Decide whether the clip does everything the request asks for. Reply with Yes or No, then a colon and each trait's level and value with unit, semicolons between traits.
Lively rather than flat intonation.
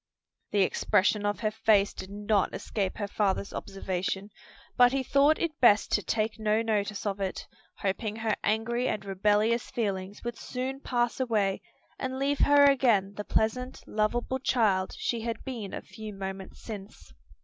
No: average, 3.3 semitones